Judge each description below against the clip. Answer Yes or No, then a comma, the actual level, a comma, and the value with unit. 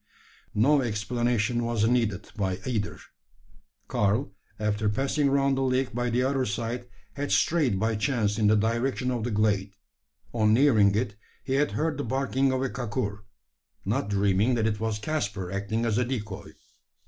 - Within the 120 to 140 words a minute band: No, average, 165 wpm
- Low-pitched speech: Yes, low, 115 Hz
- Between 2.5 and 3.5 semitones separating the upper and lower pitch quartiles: No, average, 3.9 semitones